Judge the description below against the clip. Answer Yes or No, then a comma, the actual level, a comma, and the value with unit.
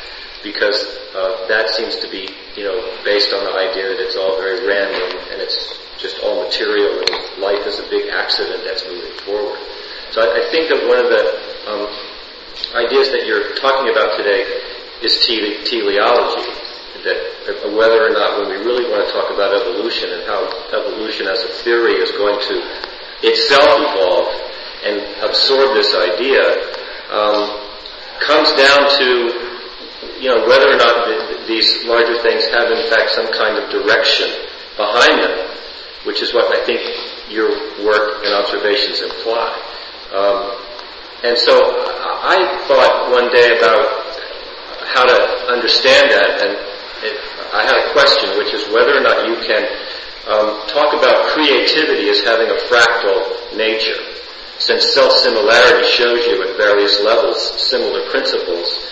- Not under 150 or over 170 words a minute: Yes, average, 155 wpm